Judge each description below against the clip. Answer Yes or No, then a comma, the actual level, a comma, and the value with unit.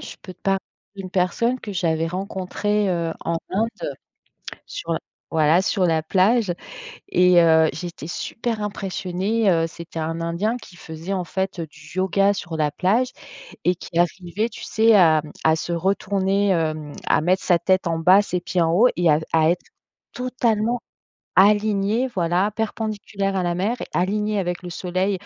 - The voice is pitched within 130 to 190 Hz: Yes, medium, 185 Hz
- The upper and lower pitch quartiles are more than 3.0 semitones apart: Yes, average, 3.4 semitones